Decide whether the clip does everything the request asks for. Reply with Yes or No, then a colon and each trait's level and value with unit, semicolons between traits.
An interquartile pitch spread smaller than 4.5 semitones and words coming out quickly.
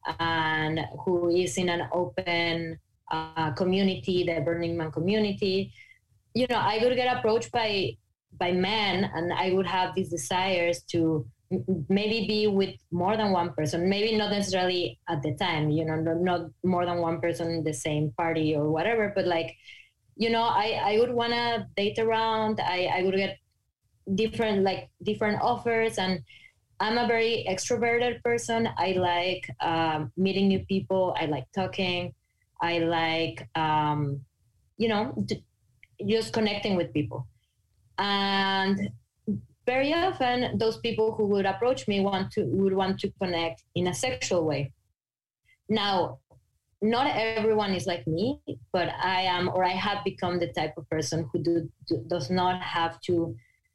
No: average, 4.1 semitones; average, 160 wpm